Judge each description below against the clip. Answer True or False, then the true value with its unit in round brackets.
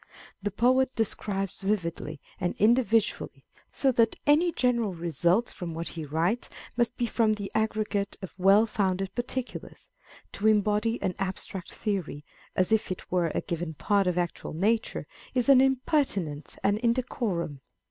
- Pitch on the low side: False (205 Hz)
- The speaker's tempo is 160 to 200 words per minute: False (145 wpm)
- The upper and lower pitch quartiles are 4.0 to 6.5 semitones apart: True (4.7 semitones)